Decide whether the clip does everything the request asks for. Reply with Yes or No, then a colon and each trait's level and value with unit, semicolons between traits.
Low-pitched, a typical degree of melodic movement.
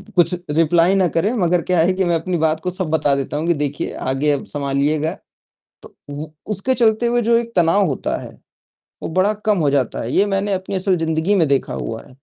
No: medium, 170 Hz; average, 4.5 semitones